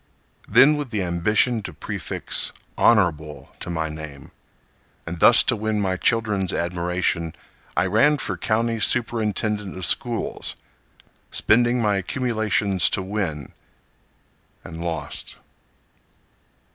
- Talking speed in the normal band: No, slow, 105 wpm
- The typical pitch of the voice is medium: No, low, 100 Hz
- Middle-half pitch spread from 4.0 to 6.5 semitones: Yes, average, 4.8 semitones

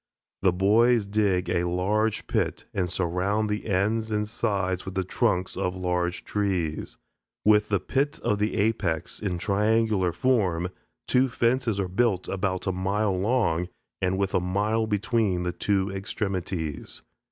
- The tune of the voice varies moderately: Yes, average, 3.0 semitones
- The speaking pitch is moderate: No, low, 100 Hz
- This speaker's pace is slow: No, average, 150 wpm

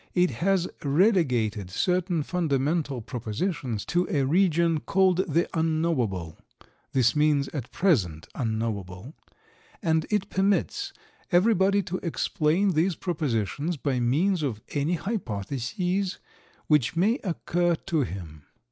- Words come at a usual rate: No, slow, 110 wpm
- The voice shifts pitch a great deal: Yes, wide, 6.5 semitones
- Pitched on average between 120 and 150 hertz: No, medium, 160 Hz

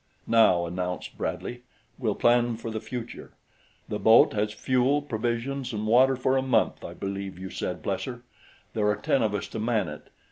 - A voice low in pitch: Yes, low, 115 Hz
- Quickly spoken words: No, average, 180 wpm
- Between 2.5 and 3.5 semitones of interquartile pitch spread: Yes, average, 3.1 semitones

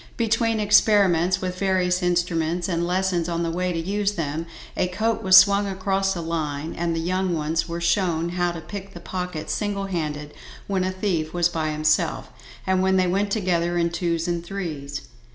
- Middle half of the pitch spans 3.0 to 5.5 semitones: No, narrow, 2.4 semitones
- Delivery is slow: No, average, 190 wpm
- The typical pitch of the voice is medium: Yes, medium, 180 Hz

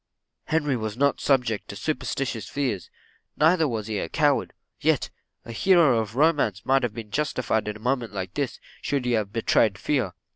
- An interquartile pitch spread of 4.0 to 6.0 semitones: Yes, average, 4.8 semitones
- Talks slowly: No, average, 180 wpm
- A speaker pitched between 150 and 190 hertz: No, low, 125 Hz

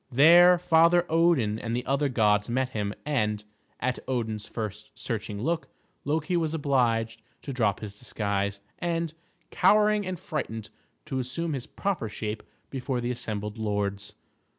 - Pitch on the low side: Yes, low, 125 Hz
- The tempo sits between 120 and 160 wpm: Yes, average, 145 wpm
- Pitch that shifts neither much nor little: No, wide, 6.9 semitones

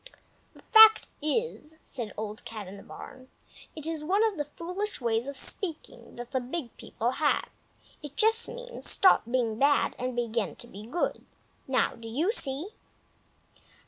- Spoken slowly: No, average, 165 wpm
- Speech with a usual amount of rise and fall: No, wide, 7.0 semitones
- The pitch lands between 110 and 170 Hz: No, very high, 280 Hz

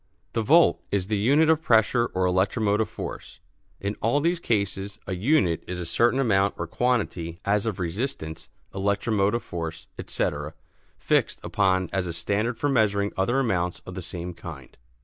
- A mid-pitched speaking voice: No, low, 100 Hz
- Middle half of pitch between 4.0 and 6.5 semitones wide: Yes, average, 4.6 semitones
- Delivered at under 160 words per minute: No, average, 165 wpm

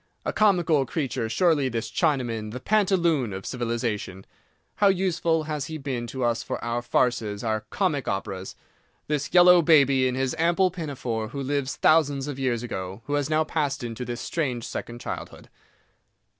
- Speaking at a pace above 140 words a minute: Yes, average, 165 wpm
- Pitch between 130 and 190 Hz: Yes, low, 135 Hz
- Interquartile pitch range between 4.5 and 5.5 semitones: Yes, average, 5.1 semitones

